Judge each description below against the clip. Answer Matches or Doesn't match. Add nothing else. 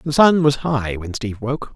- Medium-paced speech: Doesn't match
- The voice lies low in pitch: Matches